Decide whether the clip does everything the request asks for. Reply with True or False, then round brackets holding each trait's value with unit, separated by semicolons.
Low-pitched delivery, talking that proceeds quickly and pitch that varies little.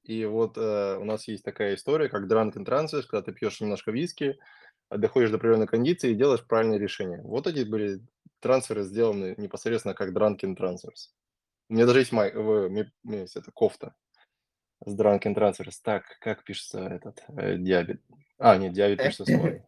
True (110 Hz; 170 wpm; 2.1 semitones)